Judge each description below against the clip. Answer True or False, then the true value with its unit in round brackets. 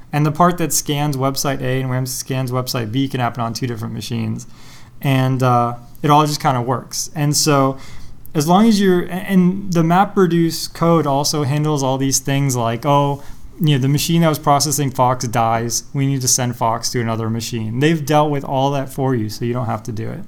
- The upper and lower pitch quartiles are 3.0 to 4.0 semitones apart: True (3.5 semitones)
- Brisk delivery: True (215 wpm)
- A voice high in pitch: False (135 Hz)